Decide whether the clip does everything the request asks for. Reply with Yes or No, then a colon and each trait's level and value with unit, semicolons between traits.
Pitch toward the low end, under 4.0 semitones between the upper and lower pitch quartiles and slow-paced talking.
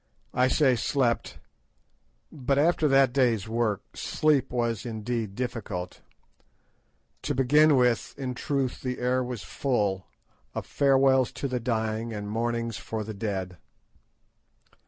Yes: low, 120 Hz; average, 3.1 semitones; slow, 130 wpm